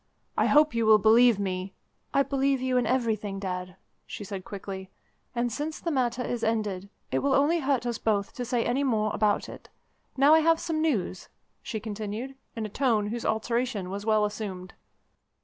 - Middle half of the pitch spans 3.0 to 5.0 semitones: Yes, average, 4.3 semitones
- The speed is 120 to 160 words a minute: No, average, 190 wpm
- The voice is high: Yes, high, 225 Hz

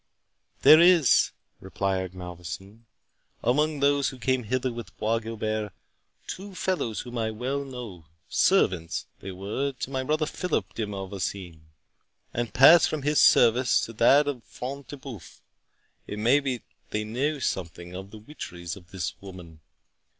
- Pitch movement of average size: No, wide, 6.1 semitones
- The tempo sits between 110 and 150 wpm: Yes, average, 145 wpm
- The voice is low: Yes, low, 115 Hz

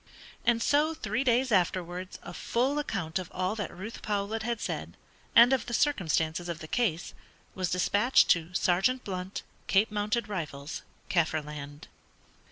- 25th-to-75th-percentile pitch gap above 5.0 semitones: Yes, wide, 5.5 semitones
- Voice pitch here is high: Yes, high, 195 Hz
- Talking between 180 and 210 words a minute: No, average, 150 wpm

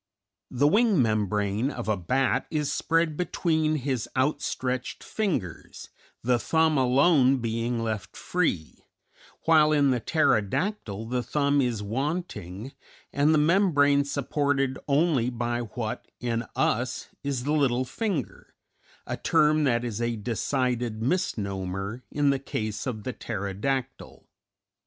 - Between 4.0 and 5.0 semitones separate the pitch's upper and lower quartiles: Yes, average, 4.5 semitones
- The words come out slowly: Yes, slow, 130 wpm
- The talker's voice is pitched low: Yes, low, 130 Hz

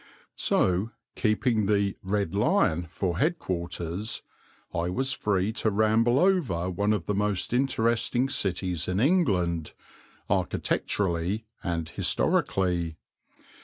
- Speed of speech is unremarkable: No, slow, 110 wpm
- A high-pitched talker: No, low, 100 Hz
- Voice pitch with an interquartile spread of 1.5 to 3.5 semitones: No, average, 4.4 semitones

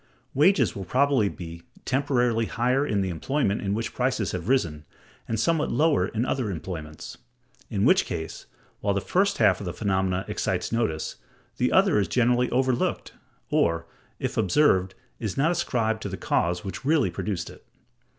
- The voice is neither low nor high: No, low, 110 Hz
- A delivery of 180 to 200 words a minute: No, average, 165 wpm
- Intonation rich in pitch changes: Yes, wide, 5.7 semitones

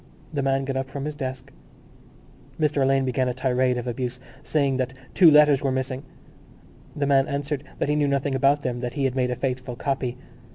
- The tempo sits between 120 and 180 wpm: No, fast, 205 wpm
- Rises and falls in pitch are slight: Yes, narrow, 1.7 semitones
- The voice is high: No, low, 135 Hz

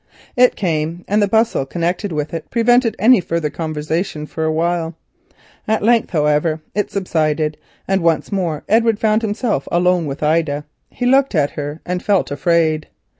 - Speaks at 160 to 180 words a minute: Yes, average, 165 wpm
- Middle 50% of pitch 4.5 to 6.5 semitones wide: Yes, average, 5.1 semitones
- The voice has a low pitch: No, medium, 170 Hz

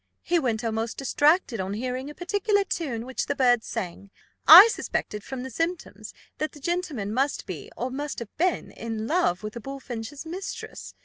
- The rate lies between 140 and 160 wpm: No, average, 180 wpm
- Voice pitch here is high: Yes, very high, 265 Hz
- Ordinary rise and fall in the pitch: No, wide, 6.4 semitones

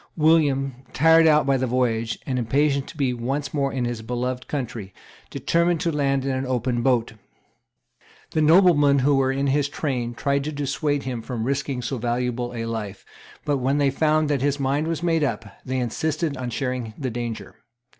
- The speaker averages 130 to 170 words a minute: No, average, 185 wpm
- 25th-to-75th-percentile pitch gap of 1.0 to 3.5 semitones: Yes, average, 3.0 semitones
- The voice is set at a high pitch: No, low, 135 Hz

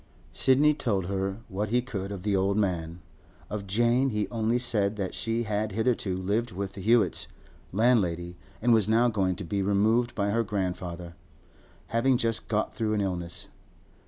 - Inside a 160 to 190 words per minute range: Yes, average, 170 wpm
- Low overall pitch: Yes, low, 105 Hz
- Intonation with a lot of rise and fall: No, average, 3.3 semitones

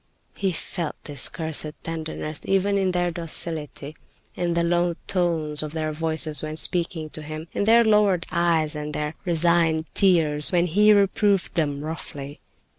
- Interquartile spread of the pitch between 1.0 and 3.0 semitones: Yes, narrow, 2.5 semitones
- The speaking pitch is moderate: Yes, medium, 165 Hz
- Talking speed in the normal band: Yes, average, 160 wpm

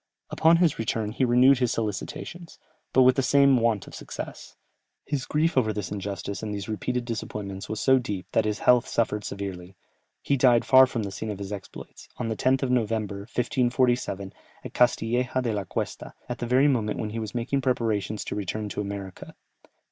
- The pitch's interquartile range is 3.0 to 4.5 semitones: Yes, average, 3.7 semitones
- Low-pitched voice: Yes, low, 115 Hz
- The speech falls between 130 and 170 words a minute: No, average, 195 wpm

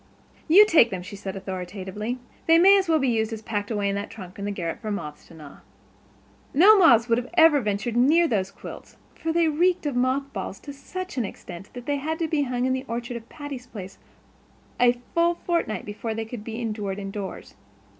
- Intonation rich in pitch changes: Yes, wide, 6.5 semitones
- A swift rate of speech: Yes, fast, 215 wpm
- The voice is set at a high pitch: Yes, high, 235 Hz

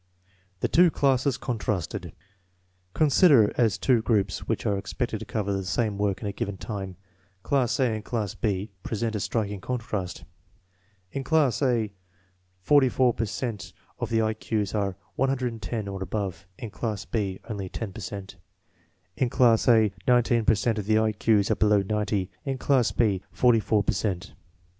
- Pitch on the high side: No, low, 110 Hz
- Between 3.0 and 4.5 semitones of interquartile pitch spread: Yes, average, 3.3 semitones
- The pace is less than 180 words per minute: Yes, average, 165 wpm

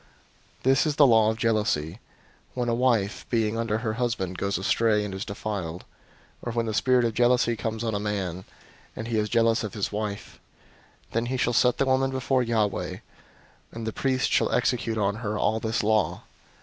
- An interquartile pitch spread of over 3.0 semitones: No, narrow, 2.4 semitones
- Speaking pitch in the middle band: No, low, 110 Hz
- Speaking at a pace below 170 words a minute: No, average, 200 wpm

